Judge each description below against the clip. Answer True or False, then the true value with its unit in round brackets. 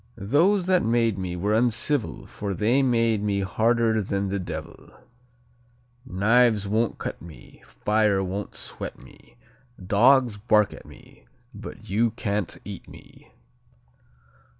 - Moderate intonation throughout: True (3.1 semitones)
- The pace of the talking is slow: True (125 wpm)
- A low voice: True (105 Hz)